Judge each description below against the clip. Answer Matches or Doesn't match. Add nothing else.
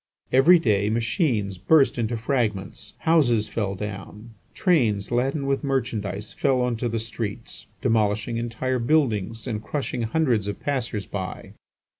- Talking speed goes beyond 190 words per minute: Doesn't match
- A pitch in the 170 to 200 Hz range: Doesn't match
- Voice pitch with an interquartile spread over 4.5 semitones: Doesn't match